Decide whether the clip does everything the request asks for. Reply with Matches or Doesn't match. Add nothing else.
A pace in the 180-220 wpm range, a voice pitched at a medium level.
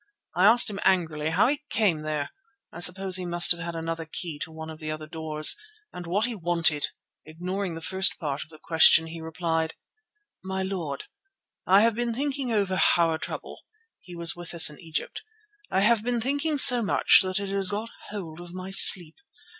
Matches